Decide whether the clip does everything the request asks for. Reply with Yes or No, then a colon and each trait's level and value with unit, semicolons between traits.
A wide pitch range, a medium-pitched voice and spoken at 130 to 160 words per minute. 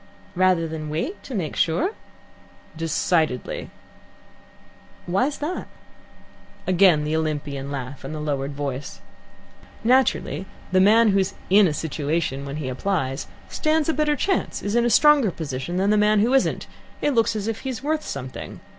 Yes: wide, 7.6 semitones; medium, 180 Hz; average, 155 wpm